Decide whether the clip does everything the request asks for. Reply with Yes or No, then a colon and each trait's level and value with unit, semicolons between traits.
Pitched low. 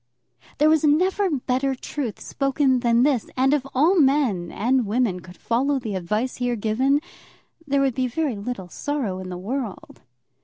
No: very high, 255 Hz